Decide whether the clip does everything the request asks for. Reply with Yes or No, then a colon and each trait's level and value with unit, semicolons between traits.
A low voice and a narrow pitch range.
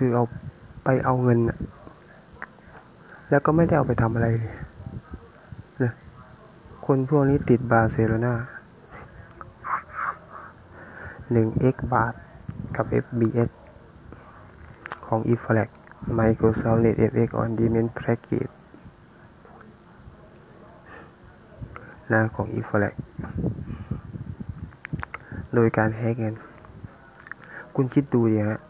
Yes: low, 115 Hz; narrow, 2.3 semitones